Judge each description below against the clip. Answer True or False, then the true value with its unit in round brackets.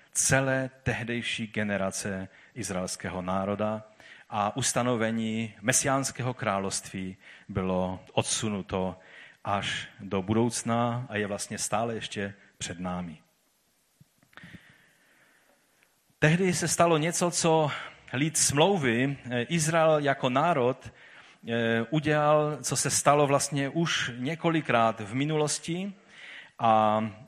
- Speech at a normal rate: False (90 wpm)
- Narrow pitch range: False (5.9 semitones)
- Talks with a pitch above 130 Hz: False (120 Hz)